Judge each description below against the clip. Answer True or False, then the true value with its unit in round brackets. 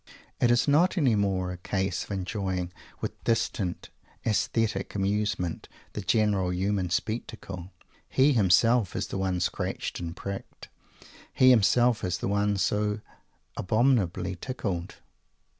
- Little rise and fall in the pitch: False (3.6 semitones)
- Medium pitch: False (100 Hz)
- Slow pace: True (125 wpm)